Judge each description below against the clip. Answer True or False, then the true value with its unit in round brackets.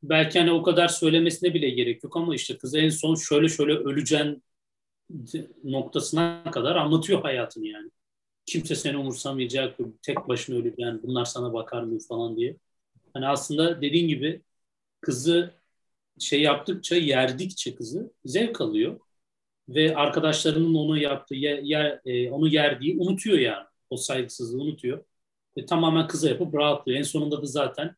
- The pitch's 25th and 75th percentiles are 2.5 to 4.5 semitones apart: True (3.7 semitones)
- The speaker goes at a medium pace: False (145 wpm)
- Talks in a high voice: False (150 Hz)